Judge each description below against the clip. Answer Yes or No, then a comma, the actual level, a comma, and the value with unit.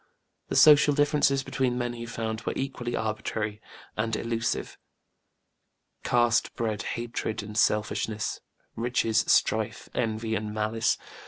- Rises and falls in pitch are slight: Yes, narrow, 1.9 semitones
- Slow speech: Yes, slow, 115 wpm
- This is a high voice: No, low, 115 Hz